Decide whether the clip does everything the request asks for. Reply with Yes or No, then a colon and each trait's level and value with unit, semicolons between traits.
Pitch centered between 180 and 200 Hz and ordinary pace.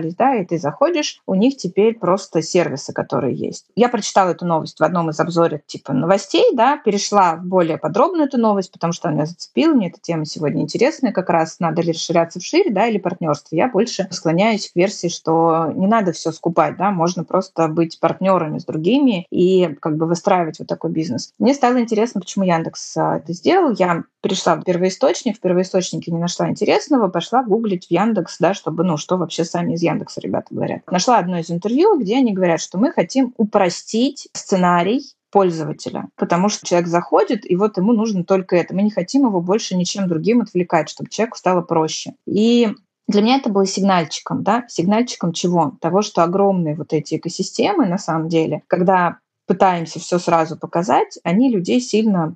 No: medium, 185 Hz; fast, 185 wpm